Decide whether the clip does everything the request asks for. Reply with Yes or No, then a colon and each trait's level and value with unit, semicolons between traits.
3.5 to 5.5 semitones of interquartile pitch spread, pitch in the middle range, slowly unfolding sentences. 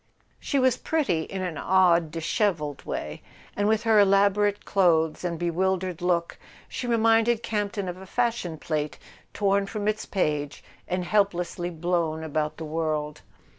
No: average, 4.2 semitones; medium, 180 Hz; average, 145 wpm